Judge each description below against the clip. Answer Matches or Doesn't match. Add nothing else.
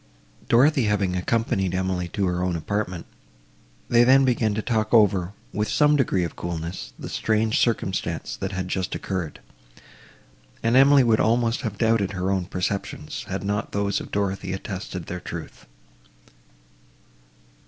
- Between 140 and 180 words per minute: Matches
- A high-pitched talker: Doesn't match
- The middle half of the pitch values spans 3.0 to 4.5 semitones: Matches